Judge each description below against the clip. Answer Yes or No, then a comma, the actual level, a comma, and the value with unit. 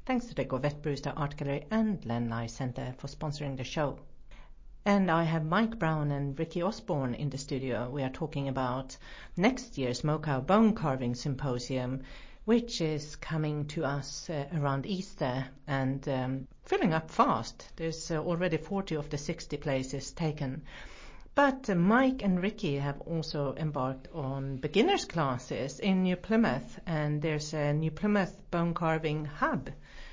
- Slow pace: No, average, 155 wpm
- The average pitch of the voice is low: No, medium, 150 Hz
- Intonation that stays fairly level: No, average, 4.9 semitones